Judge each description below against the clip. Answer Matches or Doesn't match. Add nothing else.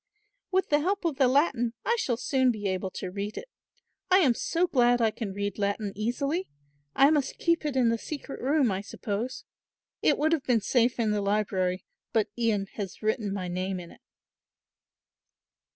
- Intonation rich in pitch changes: Matches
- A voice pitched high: Matches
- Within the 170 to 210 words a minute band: Matches